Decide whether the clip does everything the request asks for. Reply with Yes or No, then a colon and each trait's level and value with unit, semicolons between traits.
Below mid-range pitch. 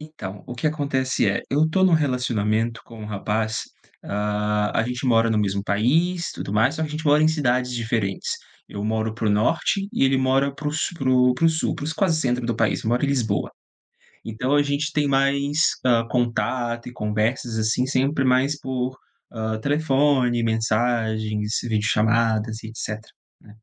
Yes: low, 120 Hz